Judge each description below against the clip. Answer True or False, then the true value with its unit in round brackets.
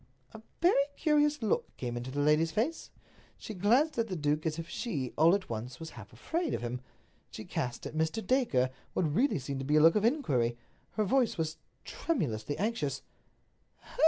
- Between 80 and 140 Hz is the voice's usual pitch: False (160 Hz)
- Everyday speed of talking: True (190 wpm)